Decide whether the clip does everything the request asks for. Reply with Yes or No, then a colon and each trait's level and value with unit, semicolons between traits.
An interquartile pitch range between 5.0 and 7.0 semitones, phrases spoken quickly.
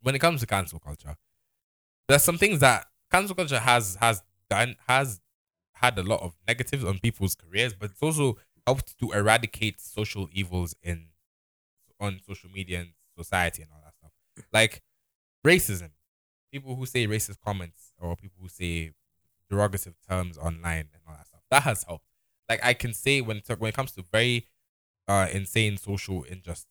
No: average, 5.3 semitones; average, 175 wpm